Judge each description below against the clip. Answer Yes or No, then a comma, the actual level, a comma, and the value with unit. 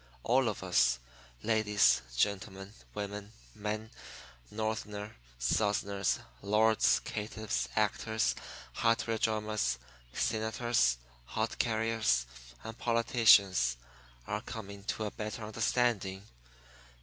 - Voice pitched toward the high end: No, low, 105 Hz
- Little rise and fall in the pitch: Yes, narrow, 1.8 semitones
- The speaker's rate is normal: No, slow, 90 wpm